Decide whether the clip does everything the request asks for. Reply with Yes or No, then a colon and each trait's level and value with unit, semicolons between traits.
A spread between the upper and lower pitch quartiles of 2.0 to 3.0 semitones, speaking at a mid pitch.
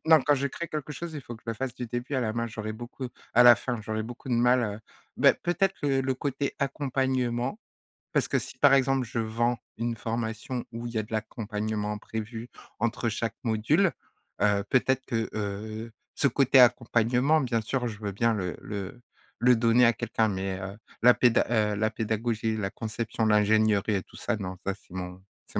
No: narrow, 2.6 semitones; low, 115 Hz